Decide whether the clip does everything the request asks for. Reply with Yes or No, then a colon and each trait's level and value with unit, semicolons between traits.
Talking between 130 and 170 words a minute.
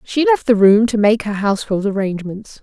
No: fast, 205 wpm